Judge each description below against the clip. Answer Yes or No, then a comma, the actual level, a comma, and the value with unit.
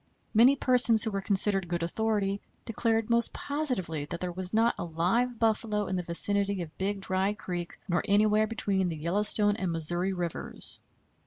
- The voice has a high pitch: Yes, high, 200 Hz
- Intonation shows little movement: No, average, 3.8 semitones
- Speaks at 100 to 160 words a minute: No, average, 170 wpm